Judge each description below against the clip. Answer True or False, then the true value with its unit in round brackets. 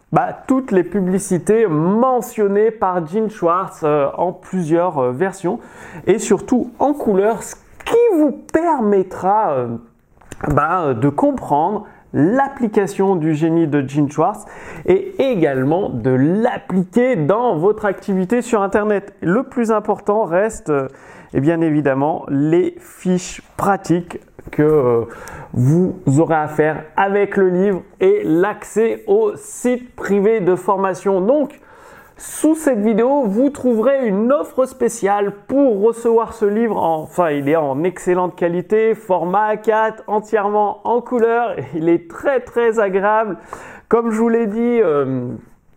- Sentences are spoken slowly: True (135 wpm)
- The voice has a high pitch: True (200 Hz)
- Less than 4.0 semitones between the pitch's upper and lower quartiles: False (5.5 semitones)